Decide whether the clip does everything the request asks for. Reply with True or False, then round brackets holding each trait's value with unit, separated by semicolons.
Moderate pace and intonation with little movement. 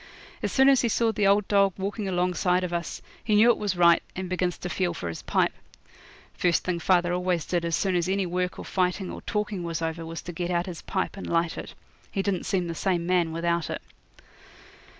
False (230 wpm; 2.3 semitones)